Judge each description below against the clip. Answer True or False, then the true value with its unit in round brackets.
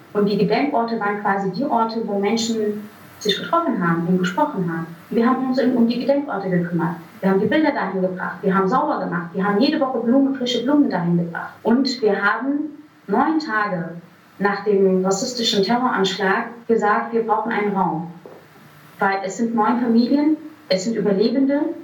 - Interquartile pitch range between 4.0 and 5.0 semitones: True (4.5 semitones)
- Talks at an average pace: True (175 wpm)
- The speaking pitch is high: True (210 Hz)